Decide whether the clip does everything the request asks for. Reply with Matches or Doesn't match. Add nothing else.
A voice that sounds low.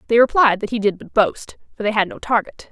Doesn't match